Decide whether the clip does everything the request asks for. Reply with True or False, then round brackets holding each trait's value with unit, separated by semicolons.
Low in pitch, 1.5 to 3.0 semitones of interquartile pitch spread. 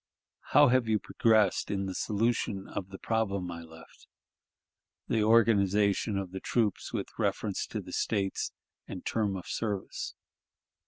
True (100 Hz; 2.7 semitones)